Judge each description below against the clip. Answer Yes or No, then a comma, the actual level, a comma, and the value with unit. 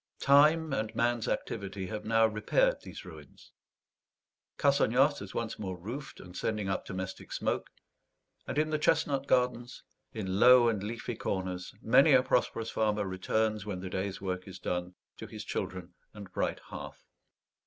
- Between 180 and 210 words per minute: No, average, 155 wpm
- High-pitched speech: No, low, 110 Hz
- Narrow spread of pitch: No, average, 4.9 semitones